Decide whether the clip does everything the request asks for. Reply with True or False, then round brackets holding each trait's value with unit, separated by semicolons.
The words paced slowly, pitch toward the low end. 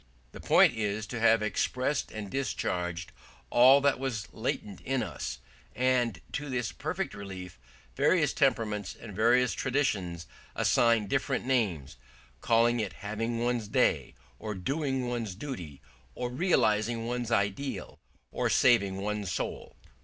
True (130 wpm; 115 Hz)